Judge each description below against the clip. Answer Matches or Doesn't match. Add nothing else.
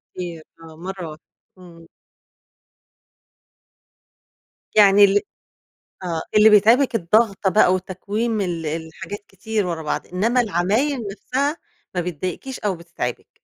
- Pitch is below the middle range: Doesn't match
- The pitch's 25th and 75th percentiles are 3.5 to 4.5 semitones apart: Matches